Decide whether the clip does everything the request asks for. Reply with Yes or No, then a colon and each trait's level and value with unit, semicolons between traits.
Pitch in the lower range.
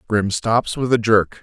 Yes: low, 110 Hz